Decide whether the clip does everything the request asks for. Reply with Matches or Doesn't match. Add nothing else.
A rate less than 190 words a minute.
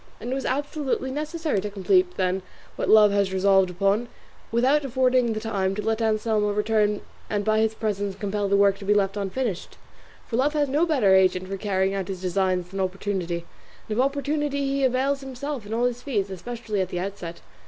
Doesn't match